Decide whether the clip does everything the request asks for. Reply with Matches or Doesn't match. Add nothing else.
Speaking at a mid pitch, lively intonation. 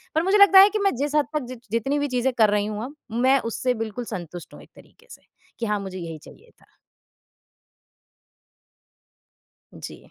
Doesn't match